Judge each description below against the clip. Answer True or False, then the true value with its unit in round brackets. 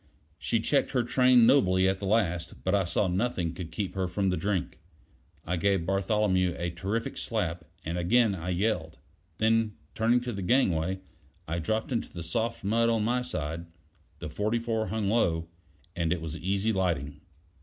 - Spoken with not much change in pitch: False (4.6 semitones)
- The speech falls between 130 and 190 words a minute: True (175 wpm)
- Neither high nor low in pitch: False (95 Hz)